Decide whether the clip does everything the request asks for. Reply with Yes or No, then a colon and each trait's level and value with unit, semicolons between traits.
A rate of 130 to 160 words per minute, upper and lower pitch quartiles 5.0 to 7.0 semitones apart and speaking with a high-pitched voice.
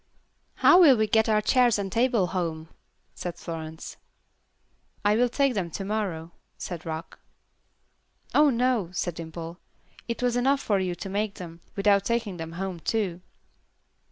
Yes: average, 155 wpm; wide, 5.5 semitones; high, 195 Hz